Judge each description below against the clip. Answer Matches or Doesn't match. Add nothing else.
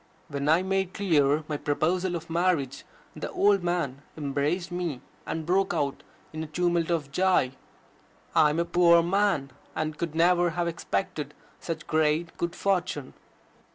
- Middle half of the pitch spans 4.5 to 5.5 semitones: Doesn't match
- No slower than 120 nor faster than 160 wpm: Matches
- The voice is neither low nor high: Matches